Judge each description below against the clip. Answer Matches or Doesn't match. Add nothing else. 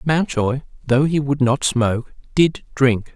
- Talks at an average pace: Matches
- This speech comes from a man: Matches